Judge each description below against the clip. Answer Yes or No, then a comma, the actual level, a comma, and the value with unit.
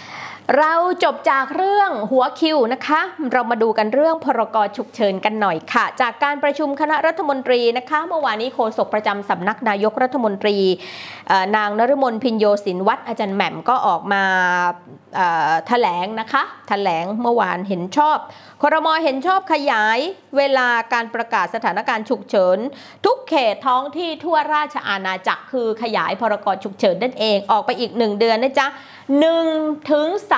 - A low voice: No, very high, 250 Hz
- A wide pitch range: Yes, wide, 5.8 semitones